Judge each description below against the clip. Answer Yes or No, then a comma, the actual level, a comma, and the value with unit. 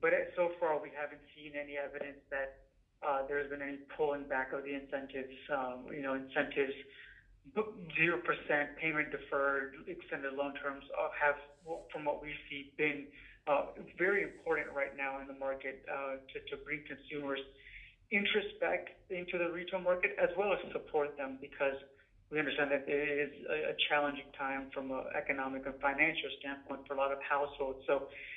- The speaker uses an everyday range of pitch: No, narrow, 1.8 semitones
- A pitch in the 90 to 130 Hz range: No, medium, 140 Hz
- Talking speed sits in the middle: Yes, average, 165 wpm